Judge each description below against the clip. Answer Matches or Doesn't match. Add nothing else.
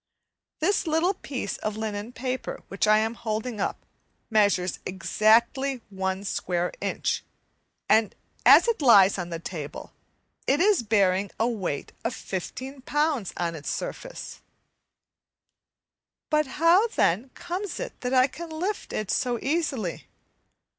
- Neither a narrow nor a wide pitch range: Doesn't match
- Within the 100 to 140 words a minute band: Matches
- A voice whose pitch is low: Doesn't match